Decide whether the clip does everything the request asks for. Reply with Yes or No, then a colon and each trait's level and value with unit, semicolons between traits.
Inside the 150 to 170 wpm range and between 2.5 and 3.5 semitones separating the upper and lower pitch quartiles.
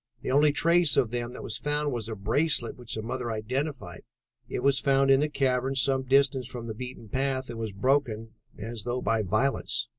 No: fast, 205 wpm; average, 3.2 semitones